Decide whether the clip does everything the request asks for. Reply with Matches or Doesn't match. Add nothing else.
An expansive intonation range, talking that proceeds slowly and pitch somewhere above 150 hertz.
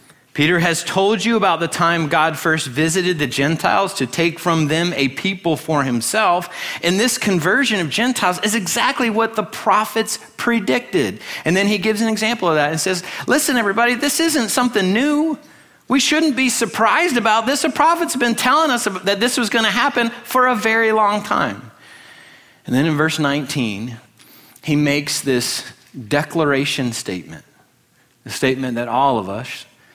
Doesn't match